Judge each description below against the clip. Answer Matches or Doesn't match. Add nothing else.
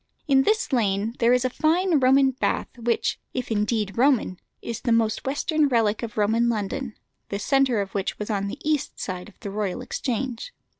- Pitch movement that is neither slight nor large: Matches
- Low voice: Doesn't match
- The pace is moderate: Matches